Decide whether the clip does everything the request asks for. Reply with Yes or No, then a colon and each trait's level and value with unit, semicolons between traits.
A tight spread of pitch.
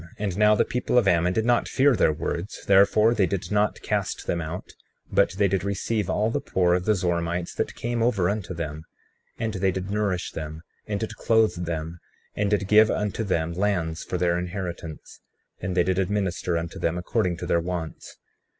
No: average, 3.3 semitones